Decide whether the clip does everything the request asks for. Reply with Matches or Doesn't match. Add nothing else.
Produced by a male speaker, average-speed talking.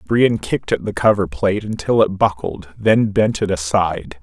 Matches